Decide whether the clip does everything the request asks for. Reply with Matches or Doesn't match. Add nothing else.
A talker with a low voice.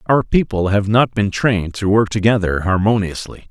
Matches